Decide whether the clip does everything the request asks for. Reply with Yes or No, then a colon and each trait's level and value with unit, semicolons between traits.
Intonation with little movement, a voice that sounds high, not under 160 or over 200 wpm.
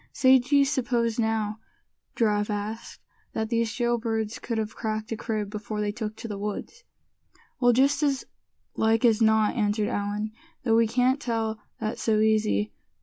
Yes: narrow, 2.0 semitones; high, 220 Hz; average, 165 wpm